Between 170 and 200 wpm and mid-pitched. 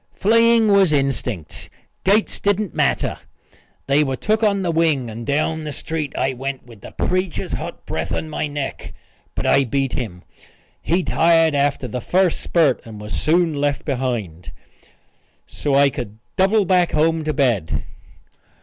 No: average, 160 wpm; medium, 145 Hz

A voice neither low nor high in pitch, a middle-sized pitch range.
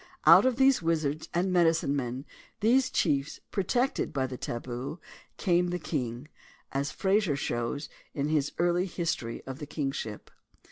Yes: medium, 155 Hz; average, 4.6 semitones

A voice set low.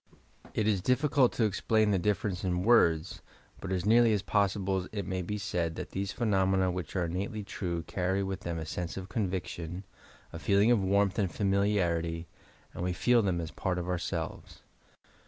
Yes: very low, 95 Hz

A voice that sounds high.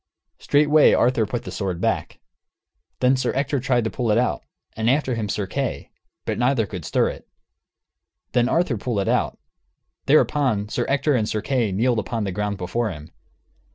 No: low, 120 Hz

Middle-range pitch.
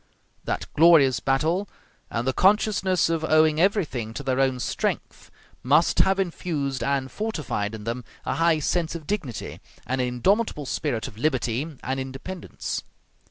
Yes: medium, 150 Hz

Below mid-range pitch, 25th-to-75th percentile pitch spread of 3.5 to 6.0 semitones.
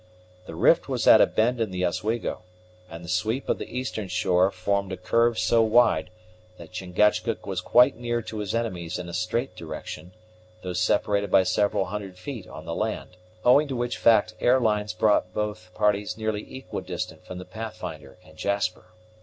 Yes: low, 100 Hz; average, 3.8 semitones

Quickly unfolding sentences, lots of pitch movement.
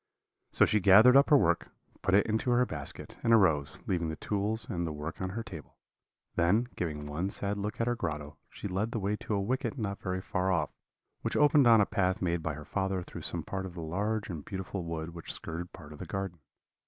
No: fast, 230 wpm; average, 4.2 semitones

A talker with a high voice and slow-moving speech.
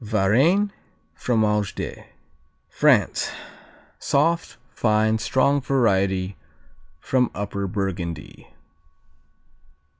No: low, 110 Hz; slow, 65 wpm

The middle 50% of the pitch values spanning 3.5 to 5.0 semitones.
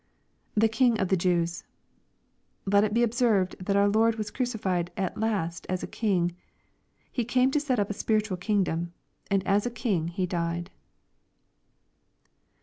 Yes: average, 3.9 semitones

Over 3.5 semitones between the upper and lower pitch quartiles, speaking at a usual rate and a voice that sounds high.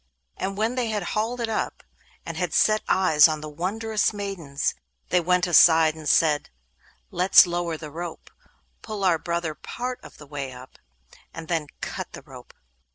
No: average, 4.9 semitones; average, 170 wpm; medium, 175 Hz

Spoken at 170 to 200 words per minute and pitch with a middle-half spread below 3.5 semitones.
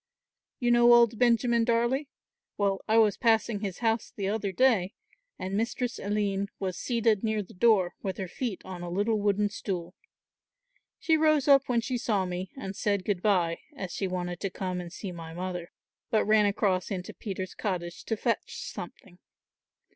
No: average, 175 wpm; average, 3.8 semitones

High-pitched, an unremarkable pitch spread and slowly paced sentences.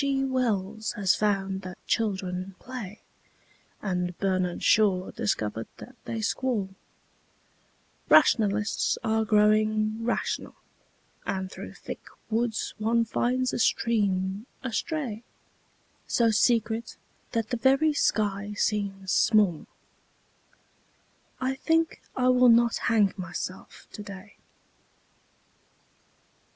Yes: high, 215 Hz; average, 3.4 semitones; slow, 95 wpm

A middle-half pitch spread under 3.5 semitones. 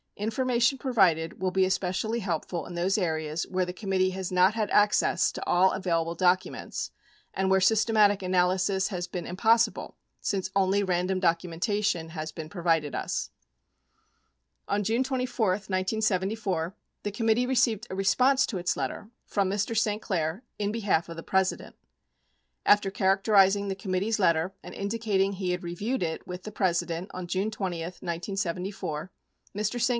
Yes: average, 2.9 semitones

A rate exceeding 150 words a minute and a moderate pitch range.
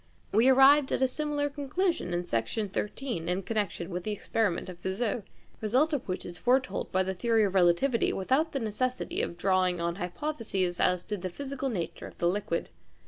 No: average, 195 wpm; wide, 6.6 semitones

